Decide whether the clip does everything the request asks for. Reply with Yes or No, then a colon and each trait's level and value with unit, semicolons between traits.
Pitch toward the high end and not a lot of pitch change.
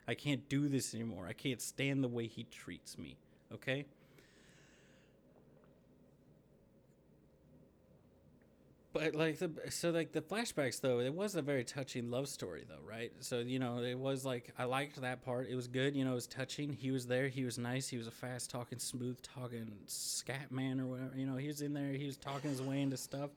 No: low, 130 Hz; narrow, 2.1 semitones